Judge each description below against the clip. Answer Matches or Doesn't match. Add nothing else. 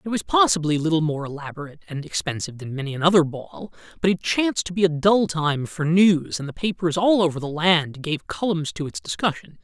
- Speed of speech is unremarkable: Doesn't match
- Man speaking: Matches